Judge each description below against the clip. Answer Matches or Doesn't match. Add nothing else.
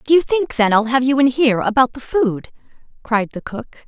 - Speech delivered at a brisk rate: Matches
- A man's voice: Doesn't match